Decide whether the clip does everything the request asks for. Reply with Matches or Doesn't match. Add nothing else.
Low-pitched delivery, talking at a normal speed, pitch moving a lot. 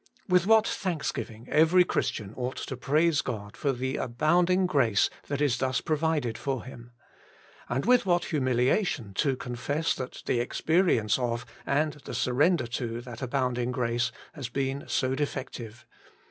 Doesn't match